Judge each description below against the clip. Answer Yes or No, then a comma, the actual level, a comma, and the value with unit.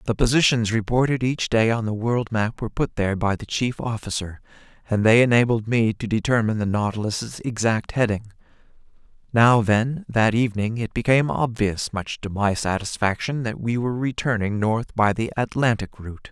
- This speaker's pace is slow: No, average, 170 wpm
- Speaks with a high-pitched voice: No, low, 115 Hz